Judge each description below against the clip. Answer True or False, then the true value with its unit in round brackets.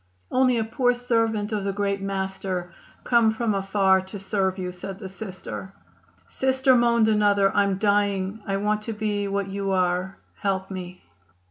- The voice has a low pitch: False (200 Hz)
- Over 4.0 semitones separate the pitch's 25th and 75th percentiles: False (2.4 semitones)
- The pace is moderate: True (160 wpm)